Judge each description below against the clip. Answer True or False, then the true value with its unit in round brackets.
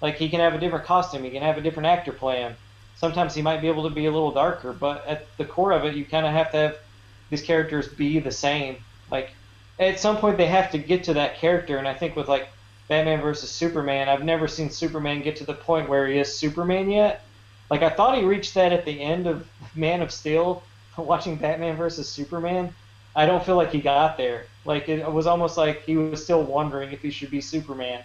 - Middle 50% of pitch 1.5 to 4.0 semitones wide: True (3.2 semitones)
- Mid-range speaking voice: True (155 Hz)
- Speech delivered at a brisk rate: True (235 wpm)